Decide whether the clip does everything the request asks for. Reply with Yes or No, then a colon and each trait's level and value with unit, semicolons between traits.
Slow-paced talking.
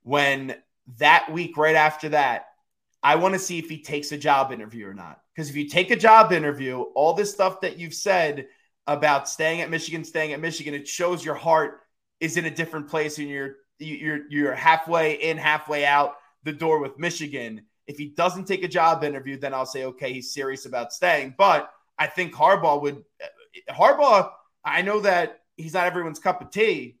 No: average, 200 wpm